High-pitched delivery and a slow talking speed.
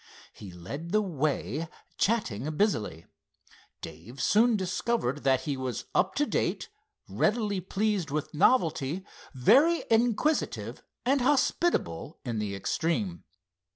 No: medium, 165 Hz; slow, 115 wpm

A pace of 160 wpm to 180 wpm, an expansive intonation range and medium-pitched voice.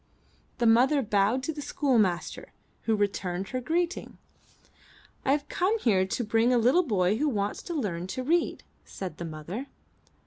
No: average, 165 wpm; wide, 6.3 semitones; high, 230 Hz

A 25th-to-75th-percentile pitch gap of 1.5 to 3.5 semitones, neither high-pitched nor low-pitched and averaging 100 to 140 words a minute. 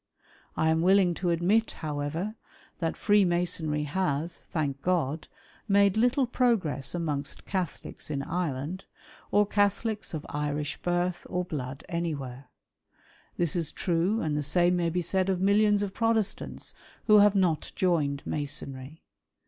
No: average, 4.7 semitones; medium, 175 Hz; slow, 135 wpm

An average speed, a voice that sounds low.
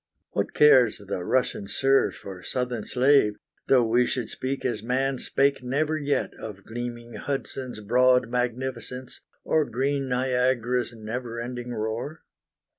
No: slow, 130 wpm; low, 125 Hz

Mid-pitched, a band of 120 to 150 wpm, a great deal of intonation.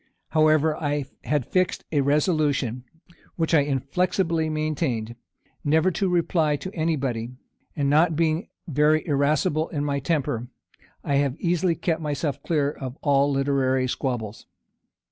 No: medium, 150 Hz; slow, 135 wpm; narrow, 2.6 semitones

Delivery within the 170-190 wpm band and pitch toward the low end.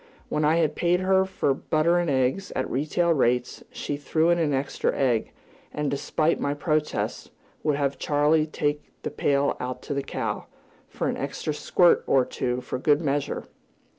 No: average, 175 wpm; medium, 145 Hz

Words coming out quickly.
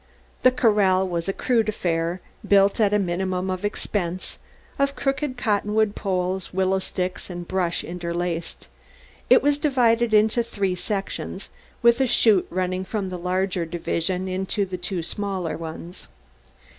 No: average, 140 wpm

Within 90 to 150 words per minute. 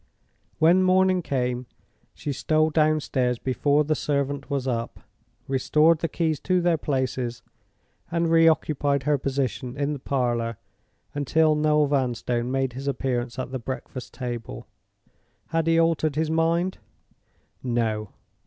Yes: slow, 135 wpm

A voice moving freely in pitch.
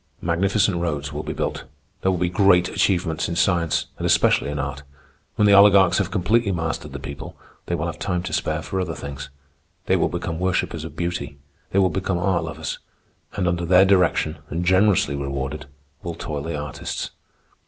No: average, 3.1 semitones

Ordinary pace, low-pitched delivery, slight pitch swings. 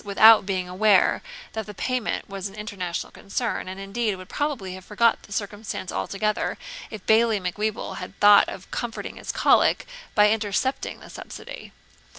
No: average, 160 wpm; high, 210 Hz; narrow, 2.2 semitones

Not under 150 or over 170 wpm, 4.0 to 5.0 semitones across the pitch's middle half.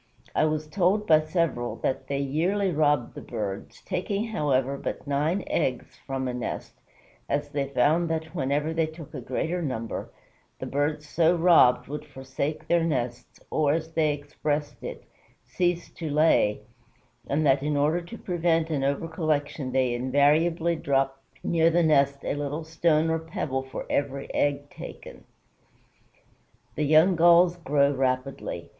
No: average, 155 wpm; average, 3.1 semitones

